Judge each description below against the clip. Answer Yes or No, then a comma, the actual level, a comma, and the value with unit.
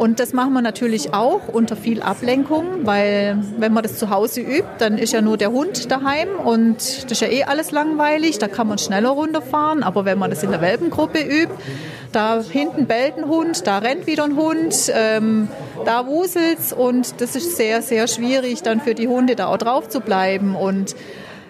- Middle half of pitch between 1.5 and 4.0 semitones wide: No, average, 5.2 semitones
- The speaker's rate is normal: No, fast, 200 wpm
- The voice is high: Yes, high, 240 Hz